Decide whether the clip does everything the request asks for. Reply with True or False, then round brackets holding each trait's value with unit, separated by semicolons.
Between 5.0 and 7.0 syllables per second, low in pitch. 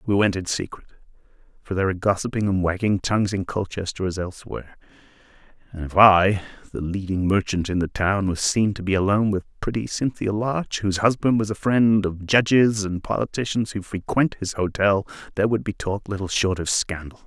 True (5.7 syllables/s; 100 Hz)